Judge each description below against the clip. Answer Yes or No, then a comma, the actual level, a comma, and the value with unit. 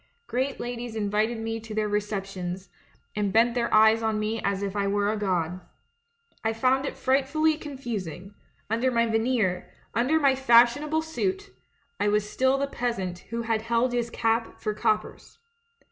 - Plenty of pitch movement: No, average, 3.5 semitones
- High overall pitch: Yes, high, 225 Hz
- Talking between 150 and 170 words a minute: Yes, average, 160 wpm